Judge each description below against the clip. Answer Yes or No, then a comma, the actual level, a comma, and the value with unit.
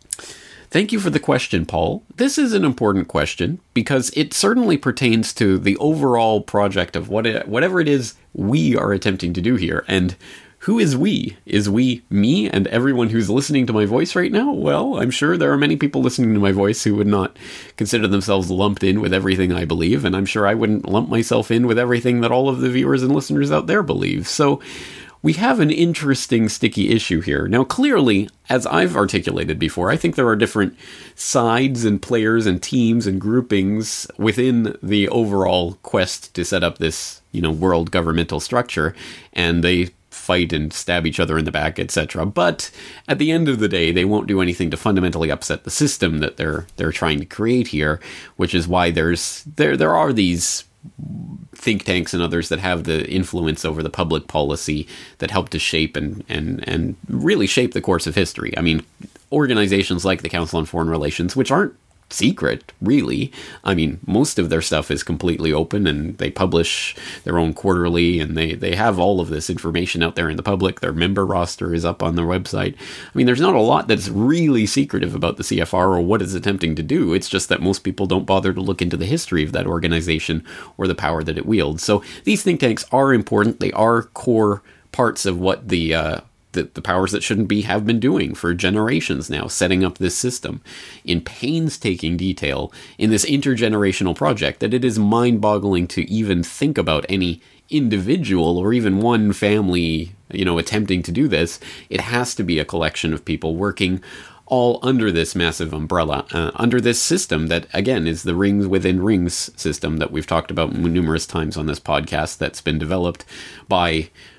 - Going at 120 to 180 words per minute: No, average, 200 wpm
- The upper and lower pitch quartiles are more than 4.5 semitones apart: Yes, average, 5.3 semitones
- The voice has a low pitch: Yes, very low, 95 Hz